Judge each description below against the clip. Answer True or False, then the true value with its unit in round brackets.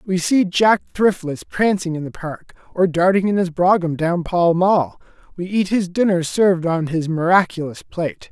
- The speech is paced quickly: False (180 wpm)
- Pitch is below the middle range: False (175 Hz)